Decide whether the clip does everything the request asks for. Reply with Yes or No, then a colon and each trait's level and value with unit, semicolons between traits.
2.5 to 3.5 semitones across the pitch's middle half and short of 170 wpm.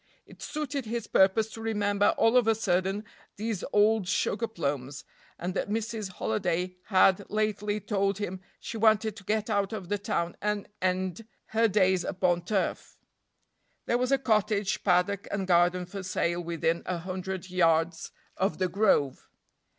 Yes: average, 3.1 semitones; average, 160 wpm